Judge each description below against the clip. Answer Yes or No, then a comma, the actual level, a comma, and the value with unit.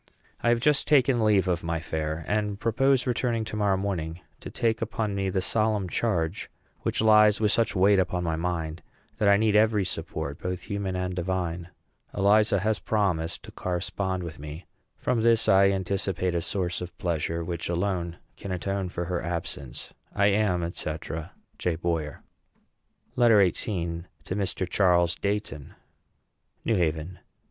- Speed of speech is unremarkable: Yes, average, 160 wpm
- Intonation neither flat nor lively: Yes, average, 3.7 semitones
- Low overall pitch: Yes, very low, 95 Hz